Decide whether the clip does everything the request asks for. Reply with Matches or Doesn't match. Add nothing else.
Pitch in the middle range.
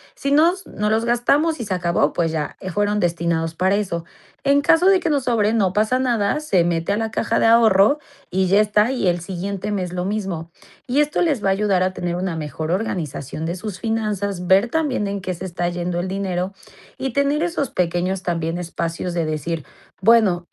Doesn't match